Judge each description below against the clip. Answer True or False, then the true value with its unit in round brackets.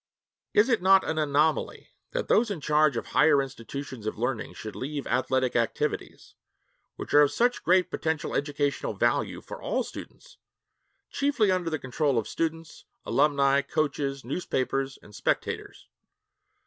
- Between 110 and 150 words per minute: True (145 wpm)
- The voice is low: False (145 Hz)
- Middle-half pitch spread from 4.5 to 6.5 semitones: False (3.3 semitones)